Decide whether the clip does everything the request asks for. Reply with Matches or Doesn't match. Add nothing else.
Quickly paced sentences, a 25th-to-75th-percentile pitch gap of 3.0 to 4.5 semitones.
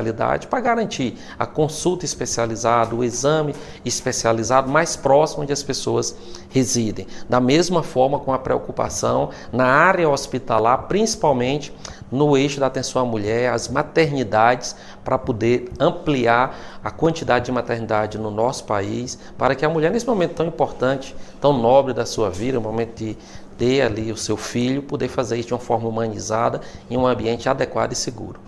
Doesn't match